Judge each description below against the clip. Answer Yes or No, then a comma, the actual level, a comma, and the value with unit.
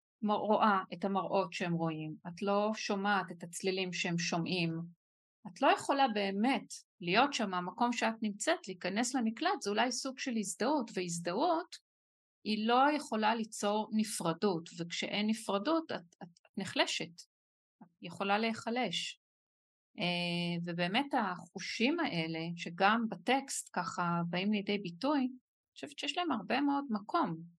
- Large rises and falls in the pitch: Yes, wide, 5.7 semitones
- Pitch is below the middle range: No, high, 205 Hz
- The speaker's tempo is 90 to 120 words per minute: No, average, 130 wpm